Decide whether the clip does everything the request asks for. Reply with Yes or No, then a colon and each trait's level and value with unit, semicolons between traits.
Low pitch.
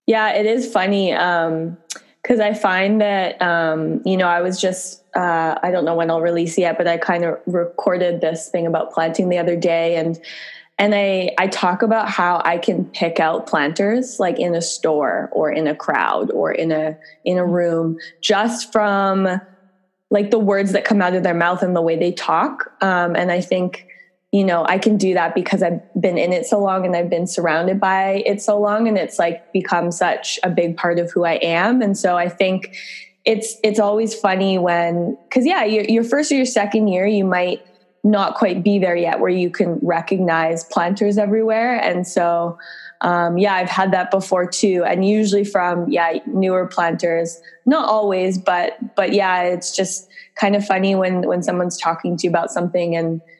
No: medium, 185 Hz